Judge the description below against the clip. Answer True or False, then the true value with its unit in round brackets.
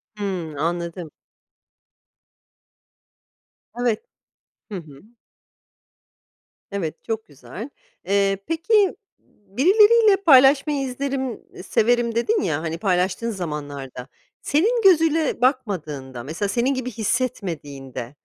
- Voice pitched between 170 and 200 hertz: False (210 Hz)